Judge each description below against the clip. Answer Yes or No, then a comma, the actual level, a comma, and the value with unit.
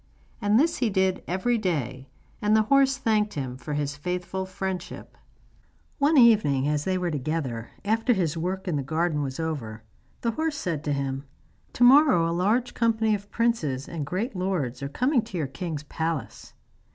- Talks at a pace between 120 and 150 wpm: No, average, 175 wpm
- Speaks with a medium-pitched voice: Yes, medium, 180 Hz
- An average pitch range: No, wide, 7.2 semitones